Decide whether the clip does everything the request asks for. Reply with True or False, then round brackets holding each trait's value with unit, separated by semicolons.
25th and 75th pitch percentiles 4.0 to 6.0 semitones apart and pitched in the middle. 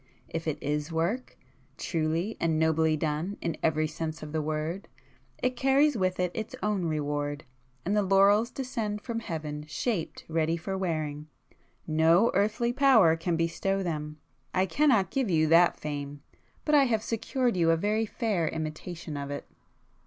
True (5.2 semitones; 170 Hz)